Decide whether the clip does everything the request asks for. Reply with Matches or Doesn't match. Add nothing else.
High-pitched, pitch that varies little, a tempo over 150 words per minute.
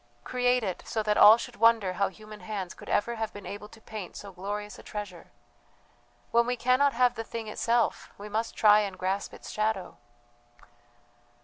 Matches